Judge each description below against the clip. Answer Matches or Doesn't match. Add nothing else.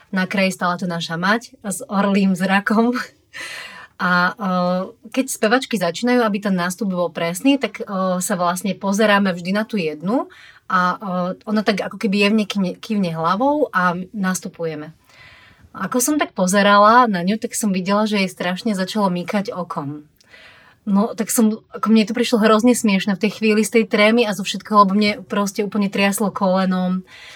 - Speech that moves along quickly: Matches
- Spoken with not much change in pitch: Doesn't match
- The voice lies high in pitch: Matches